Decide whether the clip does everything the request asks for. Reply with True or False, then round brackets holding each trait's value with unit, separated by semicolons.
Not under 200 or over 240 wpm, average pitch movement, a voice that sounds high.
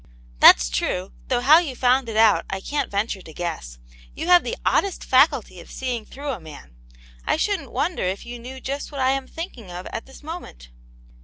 False (205 wpm; 7.1 semitones; 245 Hz)